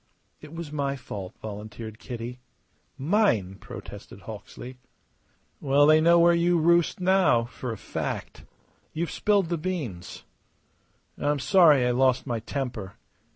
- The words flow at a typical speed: No, slow, 130 wpm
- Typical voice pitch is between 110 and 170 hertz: Yes, medium, 140 Hz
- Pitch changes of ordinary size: No, wide, 6.3 semitones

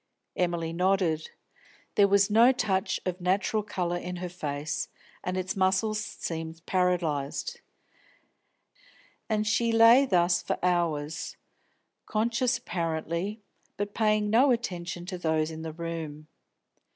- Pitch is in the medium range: Yes, medium, 180 Hz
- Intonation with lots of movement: No, average, 4.2 semitones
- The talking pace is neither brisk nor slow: No, slow, 120 wpm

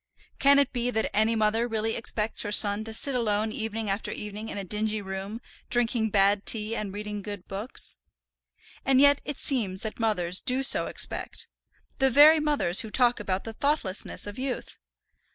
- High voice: Yes, high, 220 Hz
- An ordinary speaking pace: Yes, average, 180 wpm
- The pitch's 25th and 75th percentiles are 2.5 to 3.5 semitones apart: Yes, average, 3.1 semitones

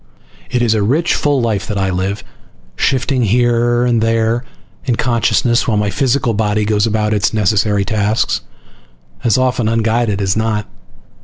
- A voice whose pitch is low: Yes, low, 110 Hz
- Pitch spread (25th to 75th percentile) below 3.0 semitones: Yes, narrow, 2.5 semitones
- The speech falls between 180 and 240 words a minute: No, average, 155 wpm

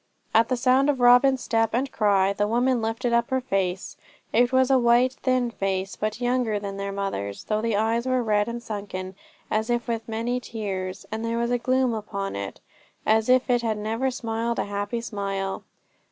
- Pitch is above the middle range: Yes, high, 225 Hz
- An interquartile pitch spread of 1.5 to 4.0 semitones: Yes, average, 3.2 semitones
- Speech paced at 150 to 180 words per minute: No, average, 195 wpm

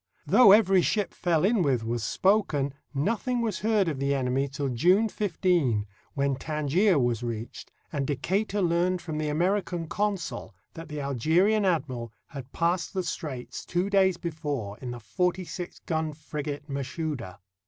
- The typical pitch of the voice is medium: Yes, medium, 160 Hz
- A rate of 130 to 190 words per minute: Yes, average, 155 wpm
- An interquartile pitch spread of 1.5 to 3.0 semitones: No, average, 5.3 semitones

